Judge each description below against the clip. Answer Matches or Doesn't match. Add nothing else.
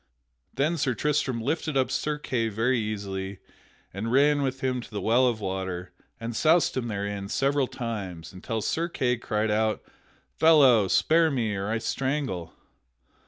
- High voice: Doesn't match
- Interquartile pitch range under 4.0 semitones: Doesn't match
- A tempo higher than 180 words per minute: Doesn't match